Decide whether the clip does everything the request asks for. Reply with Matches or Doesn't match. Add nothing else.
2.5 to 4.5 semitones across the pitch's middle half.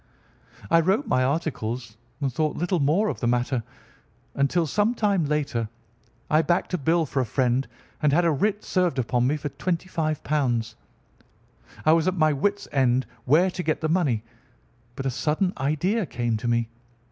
Doesn't match